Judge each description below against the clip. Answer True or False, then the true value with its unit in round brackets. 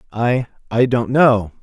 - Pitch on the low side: True (120 Hz)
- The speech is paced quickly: False (110 wpm)